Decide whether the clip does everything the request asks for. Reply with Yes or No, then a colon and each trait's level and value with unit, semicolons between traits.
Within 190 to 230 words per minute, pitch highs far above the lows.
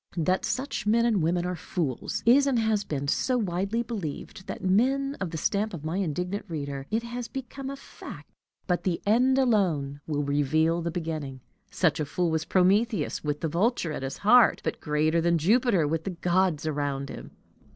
Yes: average, 195 wpm; wide, 6.3 semitones